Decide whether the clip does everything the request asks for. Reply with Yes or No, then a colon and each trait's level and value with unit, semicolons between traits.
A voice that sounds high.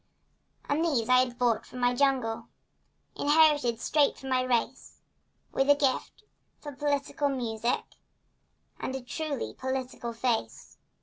Yes: very high, 260 Hz